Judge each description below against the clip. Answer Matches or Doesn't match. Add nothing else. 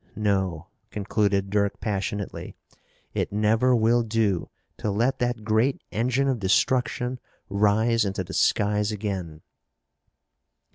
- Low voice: Matches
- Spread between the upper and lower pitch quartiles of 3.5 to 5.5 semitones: Doesn't match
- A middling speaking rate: Doesn't match